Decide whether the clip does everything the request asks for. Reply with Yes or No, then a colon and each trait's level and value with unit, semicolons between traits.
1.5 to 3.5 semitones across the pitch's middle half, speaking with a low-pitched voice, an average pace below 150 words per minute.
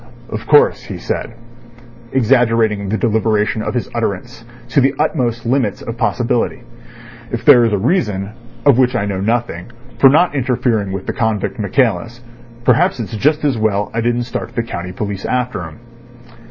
No: average, 3.1 semitones; low, 115 Hz; average, 165 wpm